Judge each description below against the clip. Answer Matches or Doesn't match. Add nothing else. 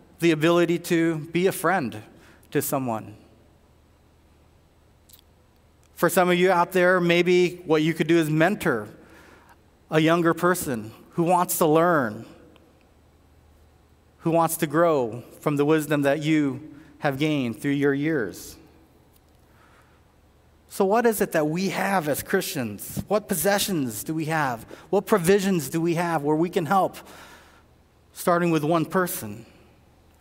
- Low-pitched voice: Doesn't match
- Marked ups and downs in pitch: Matches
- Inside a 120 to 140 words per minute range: Matches